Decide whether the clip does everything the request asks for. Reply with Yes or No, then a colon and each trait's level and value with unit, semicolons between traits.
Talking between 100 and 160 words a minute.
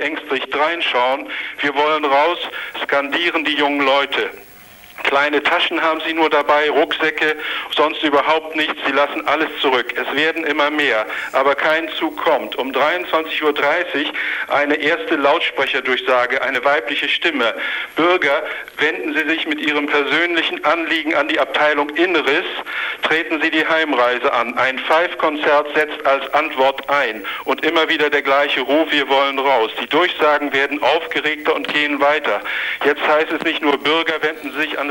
Yes: average, 150 wpm